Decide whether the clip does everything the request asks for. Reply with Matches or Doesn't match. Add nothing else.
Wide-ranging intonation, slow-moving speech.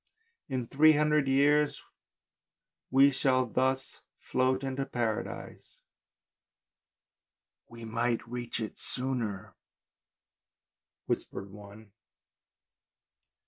Doesn't match